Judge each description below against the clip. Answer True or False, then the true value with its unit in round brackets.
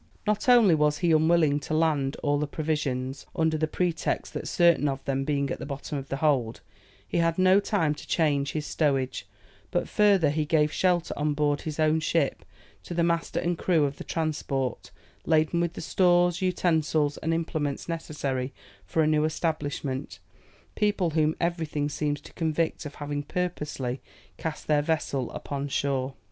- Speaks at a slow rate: False (175 wpm)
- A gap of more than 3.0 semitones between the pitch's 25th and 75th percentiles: False (2.7 semitones)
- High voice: False (155 Hz)